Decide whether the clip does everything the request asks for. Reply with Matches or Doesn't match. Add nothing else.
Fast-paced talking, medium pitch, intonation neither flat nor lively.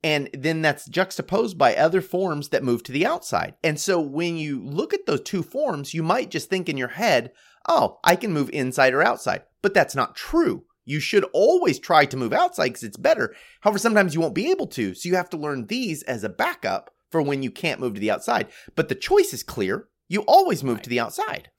Doesn't match